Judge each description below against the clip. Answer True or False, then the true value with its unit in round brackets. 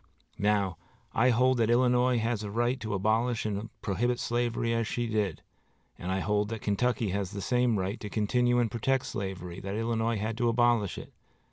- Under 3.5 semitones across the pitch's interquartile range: True (2.9 semitones)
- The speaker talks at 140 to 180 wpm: False (190 wpm)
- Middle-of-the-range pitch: False (115 Hz)